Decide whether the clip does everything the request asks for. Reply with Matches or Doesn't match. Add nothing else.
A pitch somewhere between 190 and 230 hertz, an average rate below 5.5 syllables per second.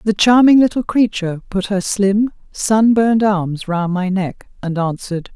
Matches